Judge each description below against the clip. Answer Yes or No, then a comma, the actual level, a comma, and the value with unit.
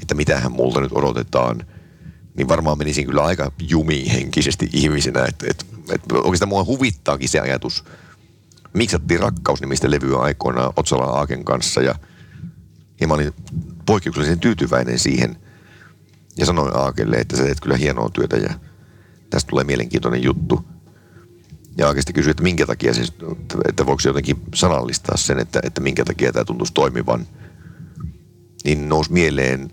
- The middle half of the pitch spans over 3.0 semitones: Yes, average, 3.6 semitones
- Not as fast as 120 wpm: No, average, 145 wpm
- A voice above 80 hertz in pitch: No, very low, 75 Hz